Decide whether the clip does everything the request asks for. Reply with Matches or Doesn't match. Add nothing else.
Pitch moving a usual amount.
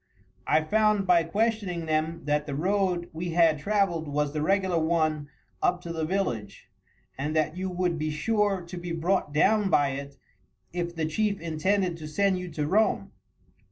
Matches